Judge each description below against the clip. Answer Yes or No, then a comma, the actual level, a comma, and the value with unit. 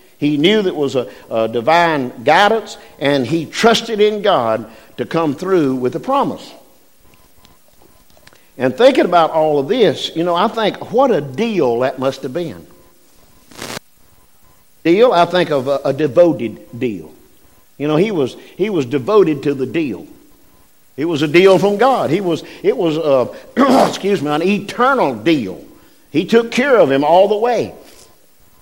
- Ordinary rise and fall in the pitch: No, wide, 7.1 semitones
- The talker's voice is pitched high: No, medium, 170 Hz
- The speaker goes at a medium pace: Yes, average, 165 wpm